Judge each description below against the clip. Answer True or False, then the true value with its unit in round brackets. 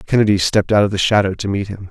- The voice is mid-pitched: False (100 Hz)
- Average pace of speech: False (285 wpm)